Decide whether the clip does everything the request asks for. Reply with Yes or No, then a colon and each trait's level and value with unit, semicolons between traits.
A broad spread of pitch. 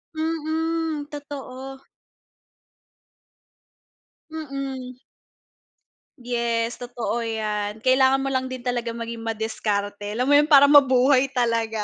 No: average, 3.2 semitones